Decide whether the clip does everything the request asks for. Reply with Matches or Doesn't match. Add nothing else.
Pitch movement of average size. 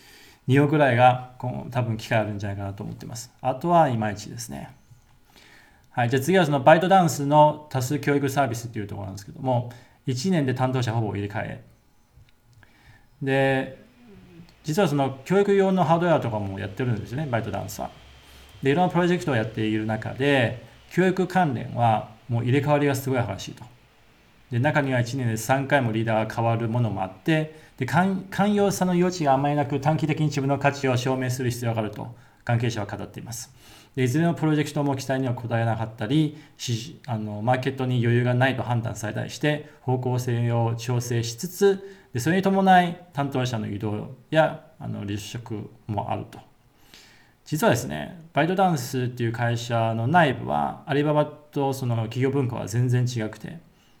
Matches